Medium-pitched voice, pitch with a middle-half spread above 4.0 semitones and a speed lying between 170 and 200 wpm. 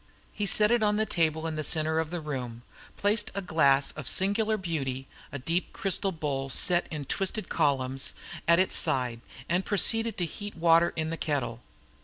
Yes: medium, 165 Hz; wide, 5.5 semitones; average, 185 wpm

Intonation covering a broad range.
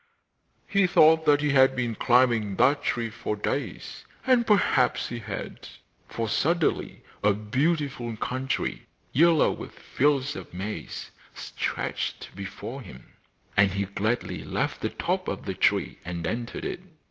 Yes: wide, 5.7 semitones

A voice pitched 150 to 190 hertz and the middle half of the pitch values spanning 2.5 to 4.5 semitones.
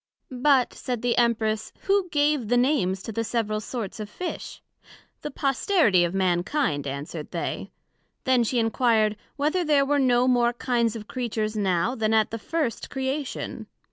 No: high, 240 Hz; average, 4.1 semitones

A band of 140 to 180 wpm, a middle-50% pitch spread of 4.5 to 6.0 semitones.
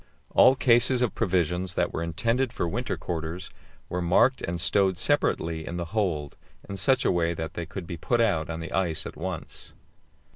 No: average, 195 wpm; average, 5.1 semitones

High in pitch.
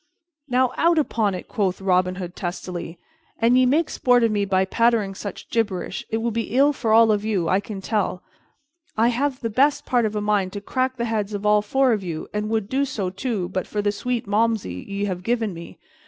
Yes: high, 210 Hz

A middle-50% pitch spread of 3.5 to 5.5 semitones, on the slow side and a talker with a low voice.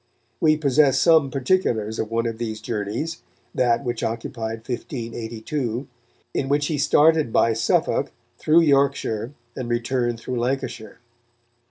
Yes: average, 3.8 semitones; slow, 130 wpm; low, 120 Hz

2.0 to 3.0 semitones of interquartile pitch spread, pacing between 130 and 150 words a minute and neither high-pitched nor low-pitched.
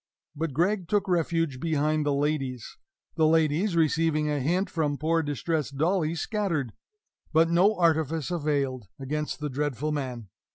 Yes: narrow, 2.6 semitones; average, 140 wpm; medium, 155 Hz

